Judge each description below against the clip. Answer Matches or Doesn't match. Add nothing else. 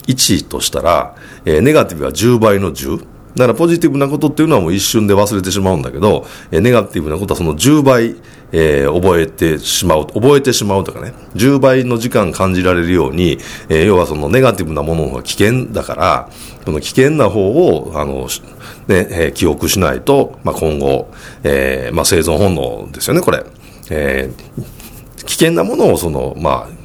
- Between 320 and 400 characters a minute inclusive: Matches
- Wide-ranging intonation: Matches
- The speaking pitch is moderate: Doesn't match